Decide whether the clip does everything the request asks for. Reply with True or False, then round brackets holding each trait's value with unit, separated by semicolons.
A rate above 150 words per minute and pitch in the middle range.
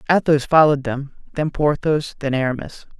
False (140 wpm; 145 Hz)